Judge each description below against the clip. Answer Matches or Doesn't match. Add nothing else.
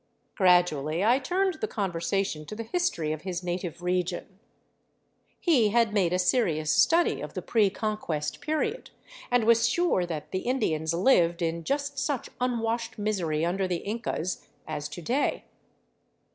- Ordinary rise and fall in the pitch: Doesn't match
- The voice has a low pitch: Doesn't match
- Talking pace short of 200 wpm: Matches